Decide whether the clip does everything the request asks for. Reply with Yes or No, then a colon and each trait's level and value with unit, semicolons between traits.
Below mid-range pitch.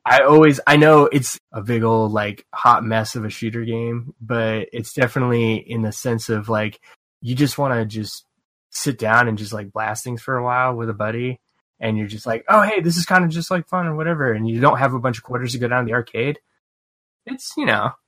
Yes: low, 120 Hz